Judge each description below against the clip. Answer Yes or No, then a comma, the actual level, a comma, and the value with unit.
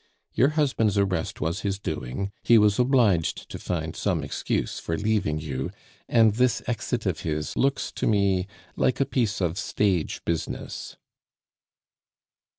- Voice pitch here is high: No, low, 100 Hz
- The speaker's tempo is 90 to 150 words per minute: Yes, average, 145 wpm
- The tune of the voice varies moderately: No, wide, 5.9 semitones